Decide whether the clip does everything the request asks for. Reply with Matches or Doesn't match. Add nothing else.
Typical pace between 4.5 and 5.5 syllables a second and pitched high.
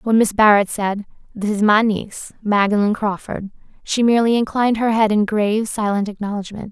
Doesn't match